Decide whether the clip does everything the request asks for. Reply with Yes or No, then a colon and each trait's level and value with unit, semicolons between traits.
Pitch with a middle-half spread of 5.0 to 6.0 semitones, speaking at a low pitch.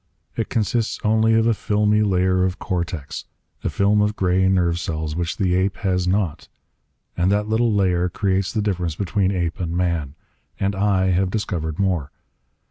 No: average, 2.8 semitones; very low, 95 Hz